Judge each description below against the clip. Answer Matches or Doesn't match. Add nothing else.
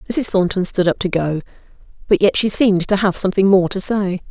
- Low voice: Doesn't match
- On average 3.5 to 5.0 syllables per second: Doesn't match